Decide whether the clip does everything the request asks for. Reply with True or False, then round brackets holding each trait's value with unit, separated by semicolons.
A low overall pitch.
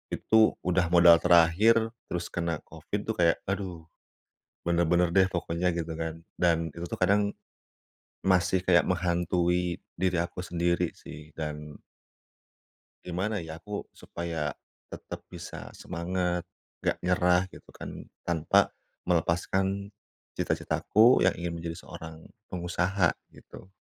True (85 Hz)